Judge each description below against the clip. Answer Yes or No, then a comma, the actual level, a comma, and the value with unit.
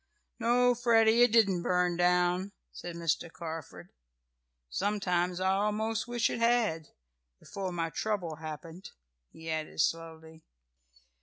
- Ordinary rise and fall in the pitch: Yes, average, 4.9 semitones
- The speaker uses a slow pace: Yes, slow, 120 wpm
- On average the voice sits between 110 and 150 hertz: No, medium, 180 Hz